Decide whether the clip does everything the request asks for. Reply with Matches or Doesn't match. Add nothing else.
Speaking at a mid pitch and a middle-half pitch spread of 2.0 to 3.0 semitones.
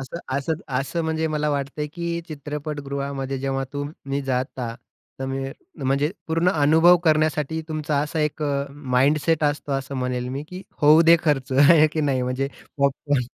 Matches